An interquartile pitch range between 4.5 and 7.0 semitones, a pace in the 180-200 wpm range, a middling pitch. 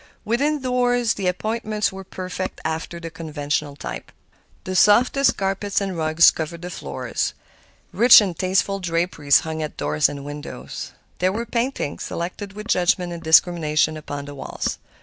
No: average, 4.8 semitones; average, 150 wpm; medium, 180 Hz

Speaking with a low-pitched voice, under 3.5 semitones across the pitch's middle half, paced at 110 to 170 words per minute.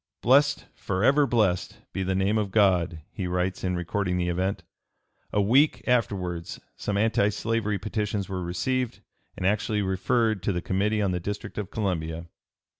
Yes: low, 100 Hz; average, 3.1 semitones; average, 160 wpm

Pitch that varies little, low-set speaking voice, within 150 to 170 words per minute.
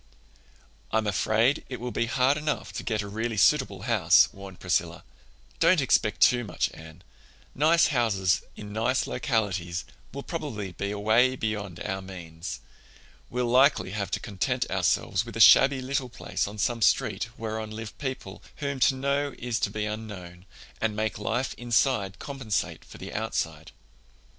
No: average, 4.3 semitones; low, 110 Hz; average, 155 wpm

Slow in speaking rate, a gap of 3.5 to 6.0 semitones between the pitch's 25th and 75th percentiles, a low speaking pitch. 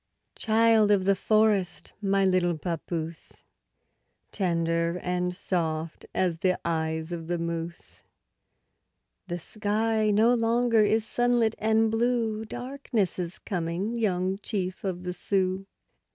No: slow, 120 wpm; average, 4.2 semitones; high, 190 Hz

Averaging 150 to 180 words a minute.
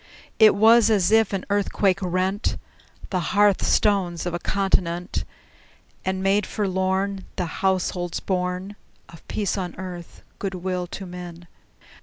No: slow, 135 wpm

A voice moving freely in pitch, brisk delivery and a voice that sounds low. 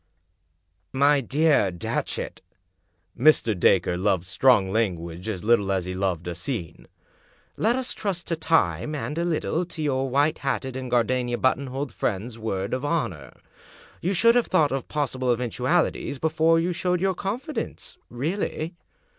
No: wide, 8.5 semitones; average, 165 wpm; low, 130 Hz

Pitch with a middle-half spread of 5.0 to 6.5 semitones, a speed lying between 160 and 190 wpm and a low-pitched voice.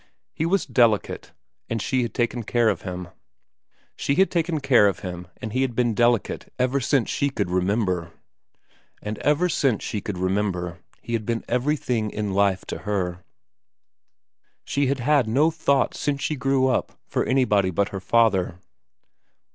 Yes: wide, 5.5 semitones; average, 165 wpm; low, 115 Hz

